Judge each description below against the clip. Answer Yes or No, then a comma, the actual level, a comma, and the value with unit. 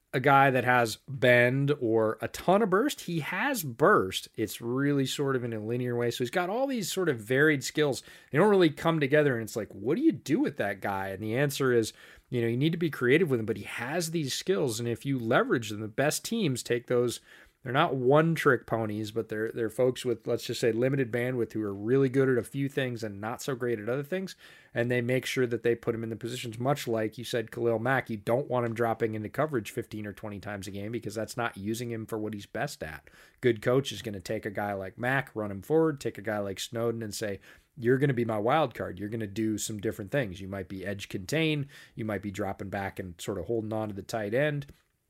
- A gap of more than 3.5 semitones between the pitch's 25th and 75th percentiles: Yes, average, 3.9 semitones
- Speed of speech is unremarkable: No, fast, 260 wpm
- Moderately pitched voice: No, low, 120 Hz